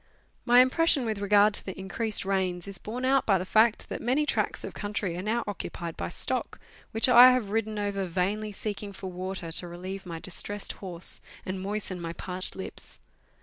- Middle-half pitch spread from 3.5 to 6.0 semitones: No, average, 2.9 semitones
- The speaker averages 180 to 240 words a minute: Yes, average, 190 wpm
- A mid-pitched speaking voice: No, high, 200 Hz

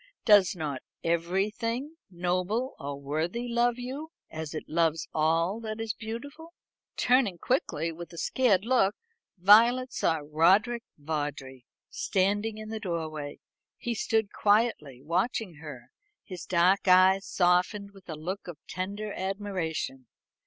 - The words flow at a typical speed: No, slow, 130 wpm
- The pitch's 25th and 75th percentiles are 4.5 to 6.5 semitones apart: Yes, wide, 5.4 semitones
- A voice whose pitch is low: No, high, 190 Hz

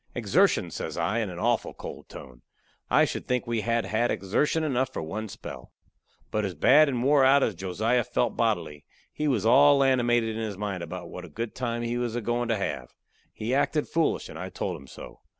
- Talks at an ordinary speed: No, fast, 215 wpm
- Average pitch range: Yes, average, 4.4 semitones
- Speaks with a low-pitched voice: Yes, low, 115 Hz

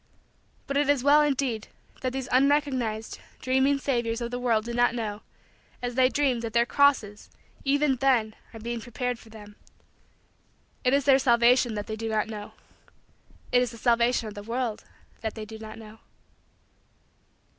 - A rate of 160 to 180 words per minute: Yes, average, 170 wpm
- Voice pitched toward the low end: No, high, 240 Hz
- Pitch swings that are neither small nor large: Yes, average, 3.0 semitones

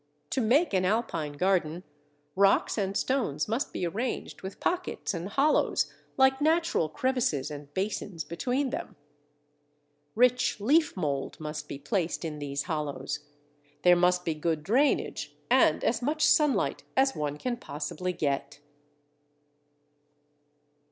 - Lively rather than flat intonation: Yes, wide, 8.6 semitones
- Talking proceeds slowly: Yes, slow, 130 wpm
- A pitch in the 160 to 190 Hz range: Yes, medium, 185 Hz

